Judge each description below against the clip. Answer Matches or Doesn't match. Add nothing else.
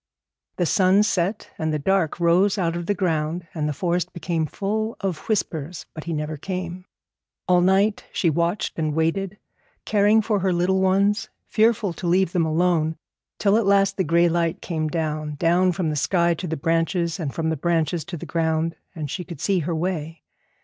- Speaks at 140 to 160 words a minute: Doesn't match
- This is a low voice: Doesn't match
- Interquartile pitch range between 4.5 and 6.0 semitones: Doesn't match